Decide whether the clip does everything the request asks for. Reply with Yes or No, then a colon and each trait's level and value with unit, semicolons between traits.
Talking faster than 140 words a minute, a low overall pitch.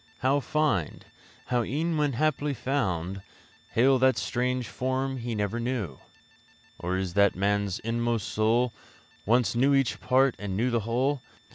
Yes: average, 150 wpm; low, 120 Hz